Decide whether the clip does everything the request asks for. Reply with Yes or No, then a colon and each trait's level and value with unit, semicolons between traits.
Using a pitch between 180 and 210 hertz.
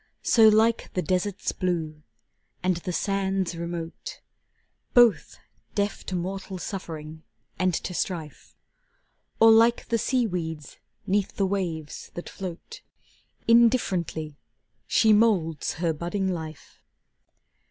Yes: medium, 185 Hz